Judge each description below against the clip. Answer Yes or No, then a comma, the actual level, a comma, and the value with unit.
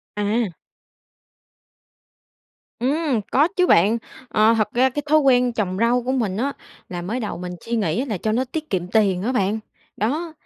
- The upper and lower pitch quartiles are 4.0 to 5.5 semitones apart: Yes, average, 4.3 semitones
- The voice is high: Yes, high, 230 Hz